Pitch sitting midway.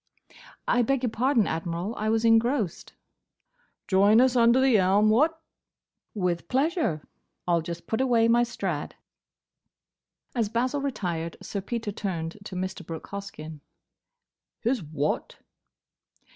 No: high, 215 Hz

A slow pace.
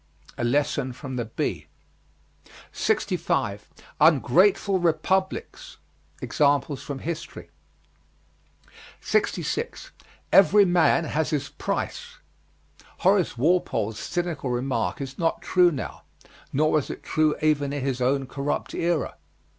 Yes: slow, 105 wpm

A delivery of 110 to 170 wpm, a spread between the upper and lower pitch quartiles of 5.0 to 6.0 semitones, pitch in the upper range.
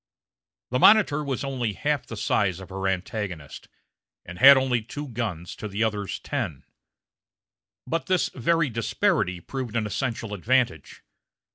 No: average, 140 wpm; average, 5.3 semitones; low, 115 Hz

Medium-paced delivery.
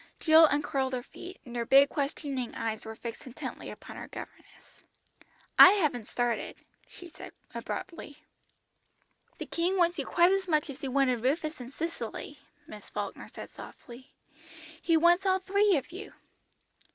Yes: average, 155 wpm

